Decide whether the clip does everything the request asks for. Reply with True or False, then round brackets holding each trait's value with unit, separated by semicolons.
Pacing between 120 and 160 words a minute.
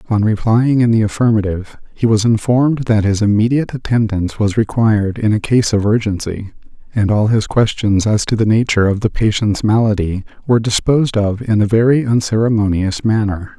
False (170 wpm)